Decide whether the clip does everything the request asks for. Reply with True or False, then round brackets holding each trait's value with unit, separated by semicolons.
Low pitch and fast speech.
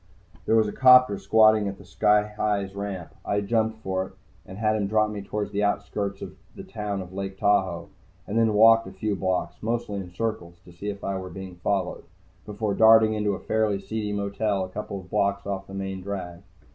True (100 Hz; 210 wpm)